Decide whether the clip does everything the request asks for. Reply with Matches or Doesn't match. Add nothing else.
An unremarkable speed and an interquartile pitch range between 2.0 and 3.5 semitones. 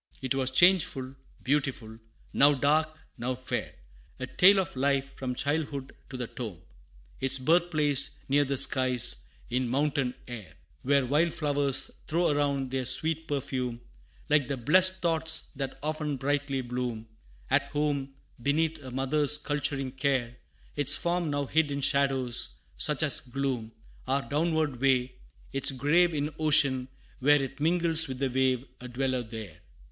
Matches